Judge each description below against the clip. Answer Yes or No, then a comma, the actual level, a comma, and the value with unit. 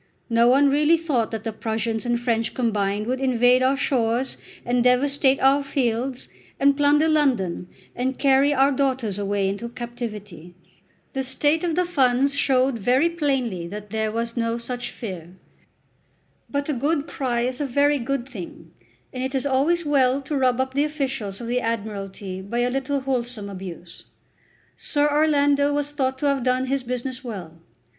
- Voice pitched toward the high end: Yes, very high, 255 Hz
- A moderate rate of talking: Yes, average, 170 wpm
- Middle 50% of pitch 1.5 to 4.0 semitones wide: Yes, average, 3.5 semitones